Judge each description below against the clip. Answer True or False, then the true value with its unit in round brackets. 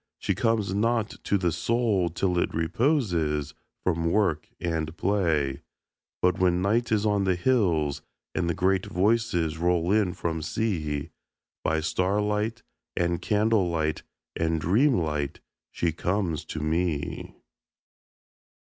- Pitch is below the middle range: True (90 Hz)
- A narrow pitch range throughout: False (4.4 semitones)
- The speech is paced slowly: True (125 wpm)